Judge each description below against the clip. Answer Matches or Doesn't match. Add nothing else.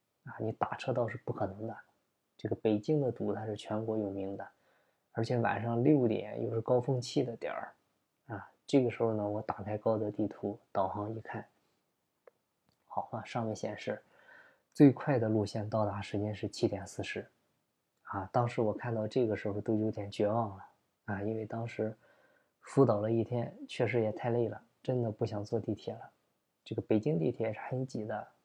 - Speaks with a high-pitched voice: Doesn't match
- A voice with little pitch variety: Matches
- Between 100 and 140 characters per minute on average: Doesn't match